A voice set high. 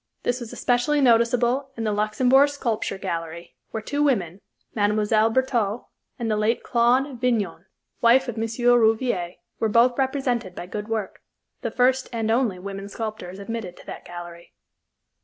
Yes: high, 230 Hz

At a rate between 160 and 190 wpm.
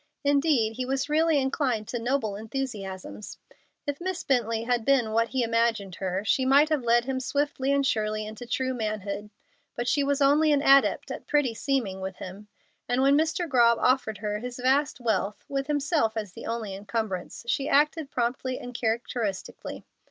Yes: average, 175 wpm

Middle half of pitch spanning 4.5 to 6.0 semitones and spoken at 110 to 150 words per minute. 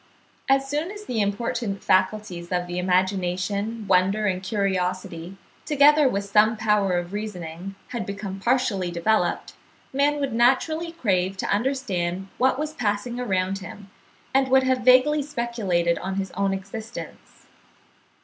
Yes: average, 5.1 semitones; average, 140 wpm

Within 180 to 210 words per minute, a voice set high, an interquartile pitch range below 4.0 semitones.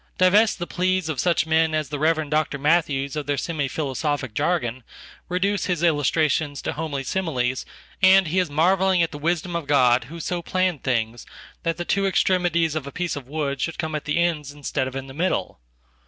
No: average, 185 wpm; medium, 155 Hz; average, 3.6 semitones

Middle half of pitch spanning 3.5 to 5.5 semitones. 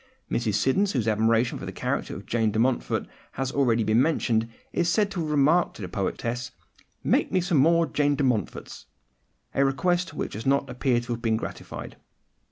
Yes: average, 5.0 semitones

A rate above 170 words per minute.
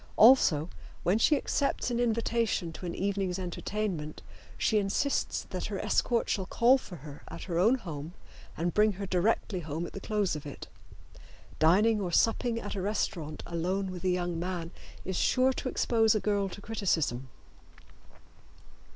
No: average, 165 wpm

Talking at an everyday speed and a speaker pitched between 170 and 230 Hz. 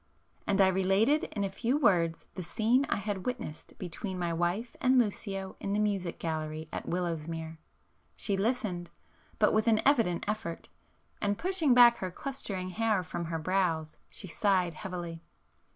Yes: average, 150 wpm; high, 190 Hz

